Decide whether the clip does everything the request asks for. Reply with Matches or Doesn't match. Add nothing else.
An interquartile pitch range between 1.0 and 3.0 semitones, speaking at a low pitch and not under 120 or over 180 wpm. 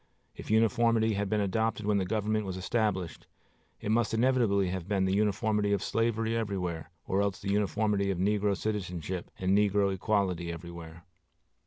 Matches